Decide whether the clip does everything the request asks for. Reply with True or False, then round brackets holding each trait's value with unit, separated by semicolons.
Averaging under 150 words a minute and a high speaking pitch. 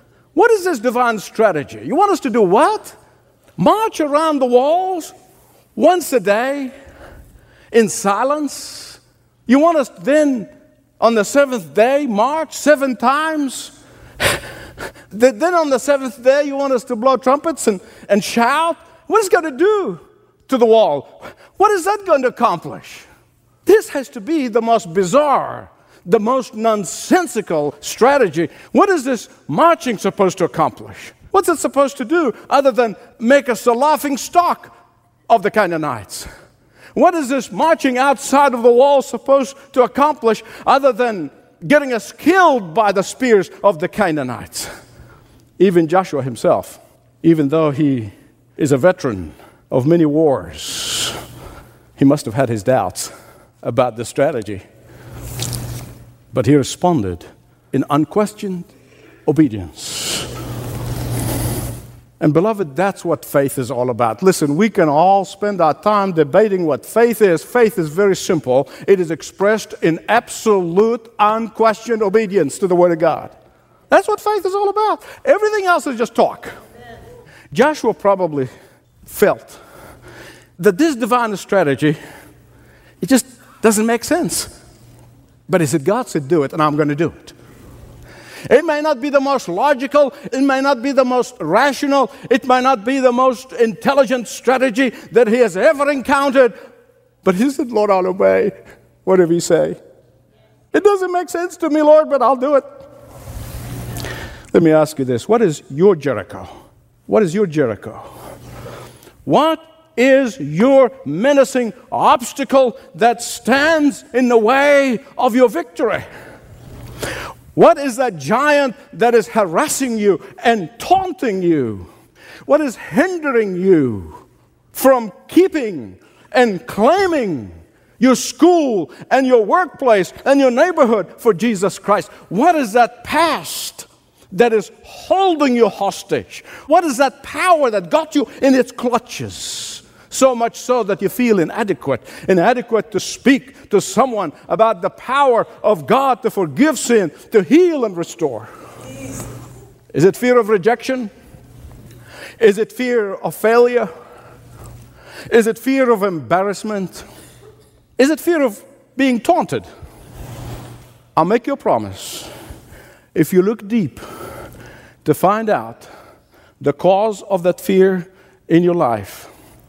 True (140 wpm; 230 Hz)